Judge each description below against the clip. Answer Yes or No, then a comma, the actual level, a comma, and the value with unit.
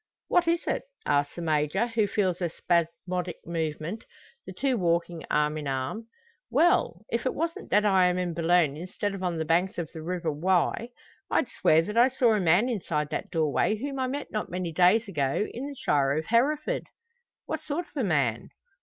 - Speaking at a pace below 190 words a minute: No, average, 200 wpm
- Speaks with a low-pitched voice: No, medium, 180 Hz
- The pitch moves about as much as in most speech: No, wide, 6.2 semitones